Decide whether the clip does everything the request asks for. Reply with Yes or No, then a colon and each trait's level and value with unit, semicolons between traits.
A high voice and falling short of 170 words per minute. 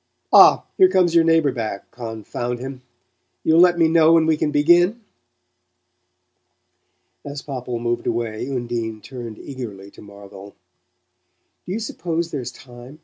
No: low, 130 Hz; average, 140 wpm